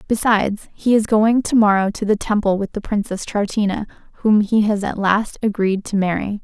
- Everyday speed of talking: Yes, average, 195 wpm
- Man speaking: No, female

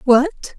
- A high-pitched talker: Yes, very high, 285 Hz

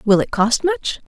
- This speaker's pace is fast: Yes, fast, 210 wpm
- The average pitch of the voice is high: Yes, high, 215 Hz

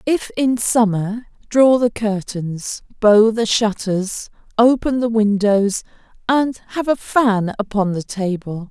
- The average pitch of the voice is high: Yes, high, 220 Hz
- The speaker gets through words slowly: Yes, slow, 130 wpm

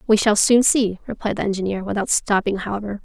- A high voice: Yes, high, 205 Hz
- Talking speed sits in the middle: Yes, average, 195 wpm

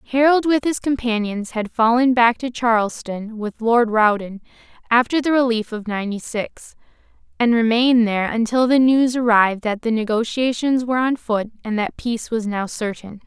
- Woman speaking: Yes, female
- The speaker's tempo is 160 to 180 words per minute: Yes, average, 165 wpm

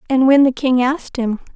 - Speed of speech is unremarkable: No, fast, 230 wpm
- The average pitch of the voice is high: Yes, very high, 260 Hz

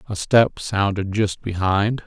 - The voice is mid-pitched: No, low, 105 Hz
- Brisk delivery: No, average, 145 wpm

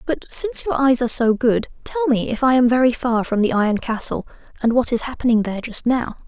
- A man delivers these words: No, female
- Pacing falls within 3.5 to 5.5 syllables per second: No, 6.1 syllables/s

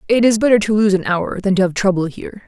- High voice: Yes, high, 200 Hz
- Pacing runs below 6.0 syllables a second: No, 6.6 syllables/s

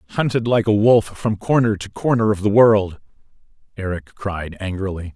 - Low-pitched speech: Yes, low, 105 Hz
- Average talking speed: Yes, average, 165 wpm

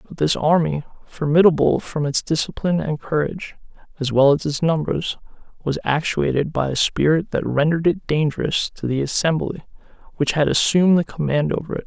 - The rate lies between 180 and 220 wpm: No, average, 165 wpm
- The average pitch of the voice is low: No, medium, 155 Hz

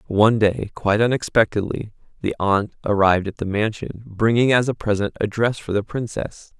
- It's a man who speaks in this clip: Yes, male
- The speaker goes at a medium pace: Yes, average, 175 wpm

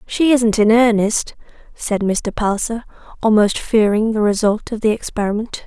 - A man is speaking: No, female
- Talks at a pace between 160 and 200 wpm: No, average, 150 wpm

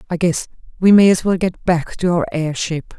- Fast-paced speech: Yes, fast, 220 wpm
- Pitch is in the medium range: Yes, medium, 175 Hz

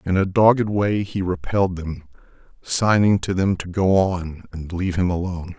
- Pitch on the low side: Yes, very low, 90 Hz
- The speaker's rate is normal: Yes, average, 185 wpm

